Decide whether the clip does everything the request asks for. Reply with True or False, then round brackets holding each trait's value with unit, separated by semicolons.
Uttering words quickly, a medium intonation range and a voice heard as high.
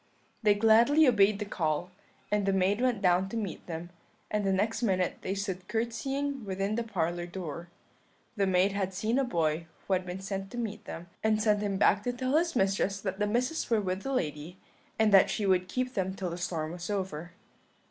True (210 wpm; 3.3 semitones; 195 Hz)